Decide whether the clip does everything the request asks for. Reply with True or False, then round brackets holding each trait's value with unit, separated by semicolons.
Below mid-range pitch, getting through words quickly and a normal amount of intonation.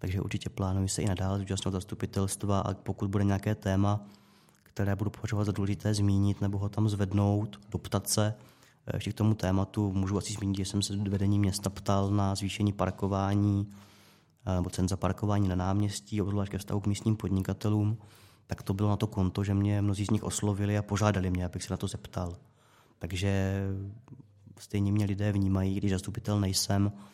False (100 Hz; 180 wpm; 1.2 semitones)